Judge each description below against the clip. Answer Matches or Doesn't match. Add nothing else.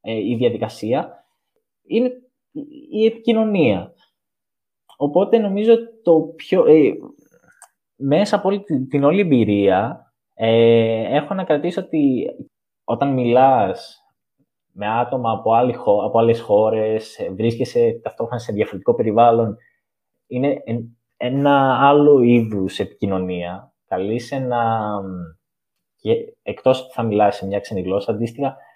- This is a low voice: Matches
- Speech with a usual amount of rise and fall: Doesn't match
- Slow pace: Matches